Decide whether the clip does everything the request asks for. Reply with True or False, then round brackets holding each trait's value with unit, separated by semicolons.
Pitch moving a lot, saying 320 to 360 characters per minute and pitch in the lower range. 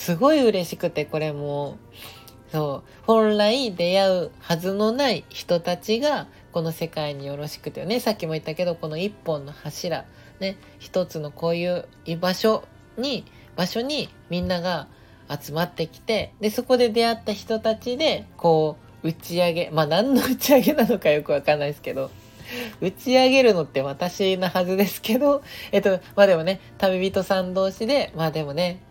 False (6.0 semitones; 330 characters per minute; 180 Hz)